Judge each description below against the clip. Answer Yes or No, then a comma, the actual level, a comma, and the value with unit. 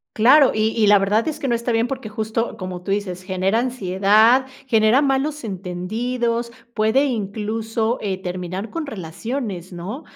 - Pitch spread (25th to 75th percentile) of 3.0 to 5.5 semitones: Yes, average, 4.0 semitones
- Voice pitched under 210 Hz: No, high, 220 Hz